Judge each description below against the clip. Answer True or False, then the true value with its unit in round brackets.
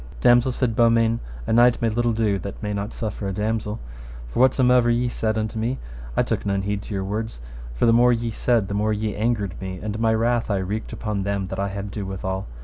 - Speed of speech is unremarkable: False (235 wpm)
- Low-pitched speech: True (110 Hz)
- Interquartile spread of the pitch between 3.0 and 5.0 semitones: False (2.6 semitones)